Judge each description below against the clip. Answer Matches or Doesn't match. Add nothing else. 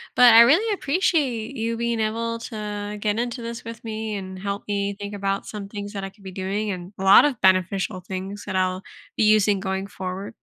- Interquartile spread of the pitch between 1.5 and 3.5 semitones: Matches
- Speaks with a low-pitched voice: Doesn't match